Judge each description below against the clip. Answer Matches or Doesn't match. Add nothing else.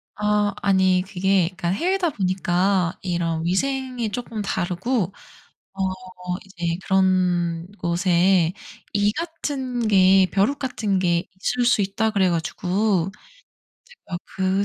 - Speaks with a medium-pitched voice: Doesn't match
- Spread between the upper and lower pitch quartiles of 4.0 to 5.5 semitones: Doesn't match